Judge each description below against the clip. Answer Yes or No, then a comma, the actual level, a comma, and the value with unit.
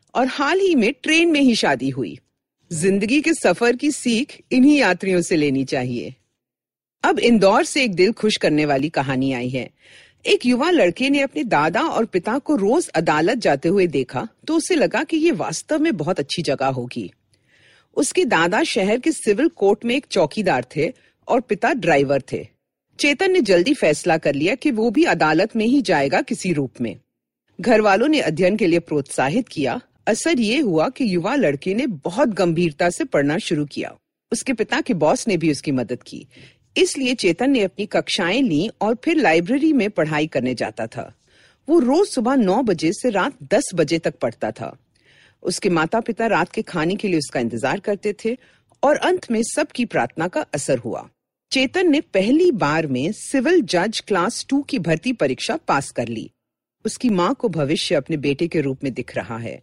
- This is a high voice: Yes, high, 215 Hz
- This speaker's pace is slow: No, fast, 190 wpm